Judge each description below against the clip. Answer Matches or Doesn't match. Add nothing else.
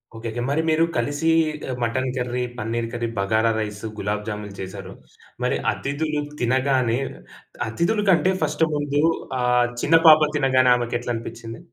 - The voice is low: Matches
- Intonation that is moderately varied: Matches